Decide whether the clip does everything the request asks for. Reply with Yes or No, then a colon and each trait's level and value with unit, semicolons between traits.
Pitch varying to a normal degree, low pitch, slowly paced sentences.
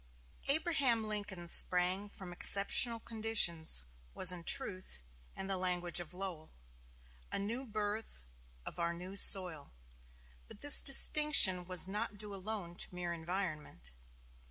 No: average, 3.6 semitones; high, 190 Hz; slow, 130 wpm